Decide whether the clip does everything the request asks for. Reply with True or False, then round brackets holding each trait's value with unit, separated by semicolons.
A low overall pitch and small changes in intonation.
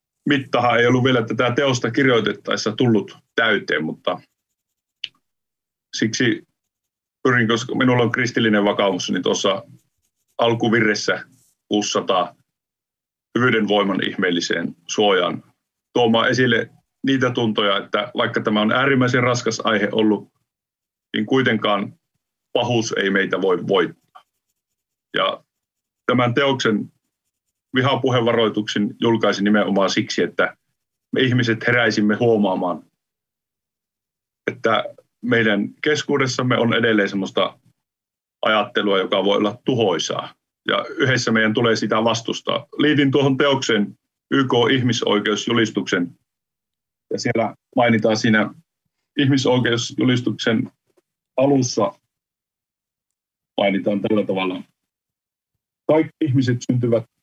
False (115 Hz; 3.2 semitones)